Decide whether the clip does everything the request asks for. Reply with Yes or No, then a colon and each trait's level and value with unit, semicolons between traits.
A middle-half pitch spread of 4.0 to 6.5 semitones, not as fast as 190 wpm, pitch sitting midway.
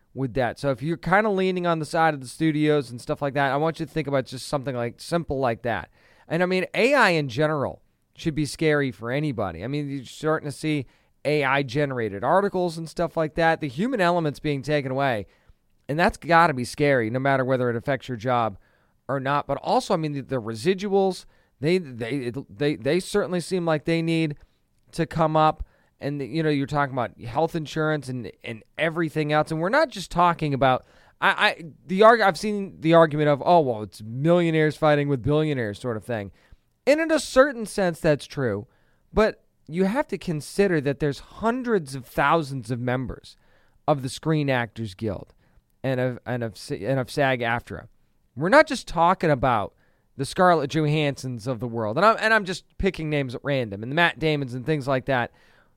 No: average, 4.5 semitones; fast, 205 wpm; medium, 150 Hz